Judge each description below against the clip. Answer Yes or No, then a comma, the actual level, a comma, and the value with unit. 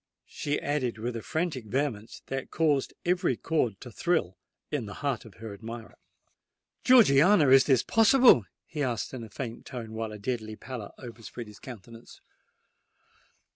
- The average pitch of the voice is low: Yes, low, 125 Hz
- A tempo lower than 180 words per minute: Yes, average, 155 wpm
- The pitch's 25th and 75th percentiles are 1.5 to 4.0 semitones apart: No, average, 4.6 semitones